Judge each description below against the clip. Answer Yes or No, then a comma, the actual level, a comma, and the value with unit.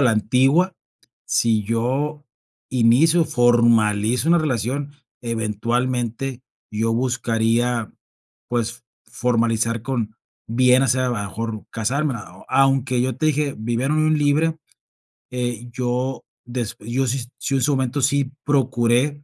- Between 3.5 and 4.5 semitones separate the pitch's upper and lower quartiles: No, average, 2.9 semitones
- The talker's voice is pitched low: Yes, low, 125 Hz